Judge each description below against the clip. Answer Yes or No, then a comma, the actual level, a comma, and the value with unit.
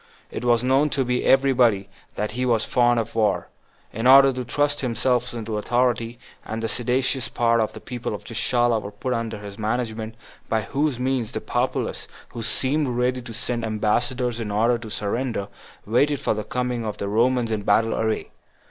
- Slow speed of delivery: No, average, 185 wpm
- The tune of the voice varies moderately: No, narrow, 2.3 semitones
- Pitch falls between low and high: No, low, 120 Hz